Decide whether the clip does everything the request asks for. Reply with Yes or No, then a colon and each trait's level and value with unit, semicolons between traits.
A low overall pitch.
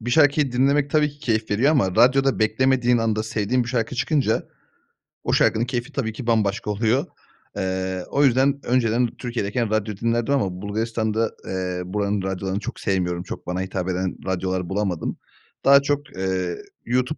Yes: low, 110 Hz